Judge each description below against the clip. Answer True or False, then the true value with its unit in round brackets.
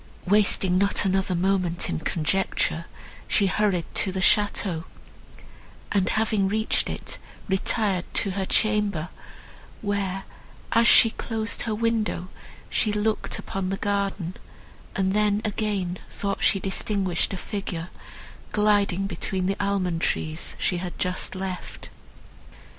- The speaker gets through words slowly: True (125 wpm)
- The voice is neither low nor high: False (195 Hz)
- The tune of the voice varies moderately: False (2.2 semitones)